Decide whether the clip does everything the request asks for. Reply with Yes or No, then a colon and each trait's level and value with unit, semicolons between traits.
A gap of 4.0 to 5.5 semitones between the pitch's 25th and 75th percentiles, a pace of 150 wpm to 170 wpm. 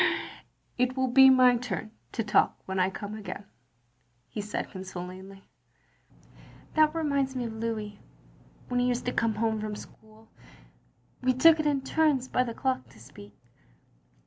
Yes: average, 4.5 semitones; average, 165 wpm